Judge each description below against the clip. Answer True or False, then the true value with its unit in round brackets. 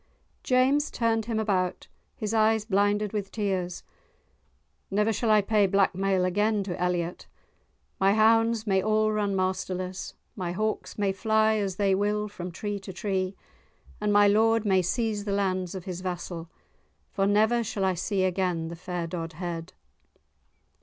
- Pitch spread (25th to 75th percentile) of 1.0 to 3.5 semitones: True (2.7 semitones)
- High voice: True (200 Hz)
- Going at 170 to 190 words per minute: False (155 wpm)